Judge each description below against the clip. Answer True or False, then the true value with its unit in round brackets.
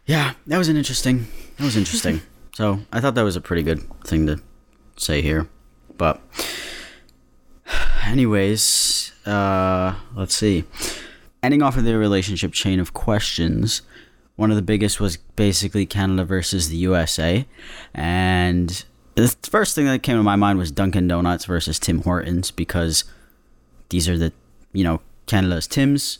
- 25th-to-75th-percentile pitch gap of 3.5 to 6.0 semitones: True (4.4 semitones)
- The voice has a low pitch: True (95 Hz)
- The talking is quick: False (150 wpm)